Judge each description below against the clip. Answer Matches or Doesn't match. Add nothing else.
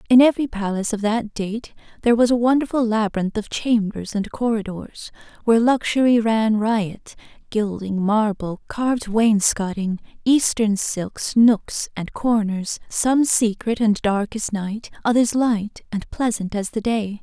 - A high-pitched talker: Matches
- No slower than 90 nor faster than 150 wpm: Matches